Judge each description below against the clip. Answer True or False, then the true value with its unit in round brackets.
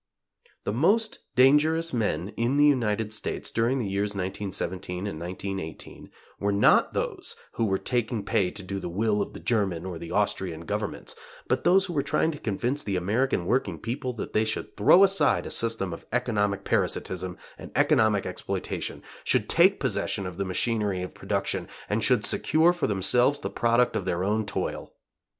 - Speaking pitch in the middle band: False (105 Hz)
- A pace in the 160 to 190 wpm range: True (175 wpm)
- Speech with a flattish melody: False (4.4 semitones)